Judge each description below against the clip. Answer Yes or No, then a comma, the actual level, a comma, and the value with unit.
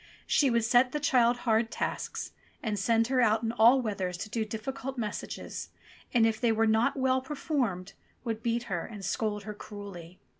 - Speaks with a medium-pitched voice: No, high, 225 Hz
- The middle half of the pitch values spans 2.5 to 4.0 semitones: Yes, average, 2.8 semitones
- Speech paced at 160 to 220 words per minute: Yes, average, 185 wpm